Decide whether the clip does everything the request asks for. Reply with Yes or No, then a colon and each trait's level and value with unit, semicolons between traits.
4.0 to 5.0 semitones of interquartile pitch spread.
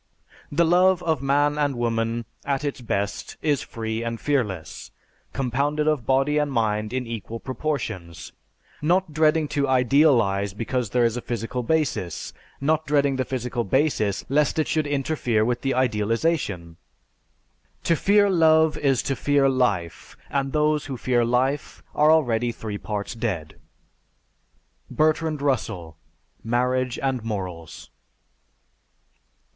Yes: average, 4.5 semitones